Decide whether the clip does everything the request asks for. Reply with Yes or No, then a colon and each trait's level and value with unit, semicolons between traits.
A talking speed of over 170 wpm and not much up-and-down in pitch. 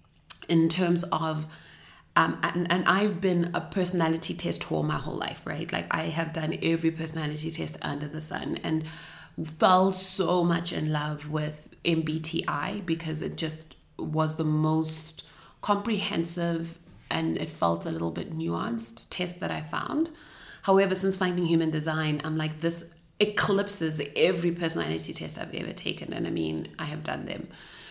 No: average, 160 wpm; narrow, 2.2 semitones